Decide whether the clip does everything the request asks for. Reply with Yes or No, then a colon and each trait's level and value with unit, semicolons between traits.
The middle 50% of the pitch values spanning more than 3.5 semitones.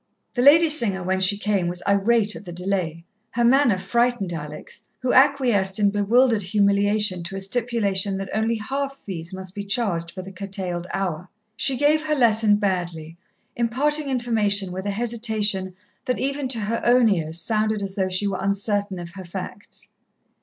Yes: average, 3.9 semitones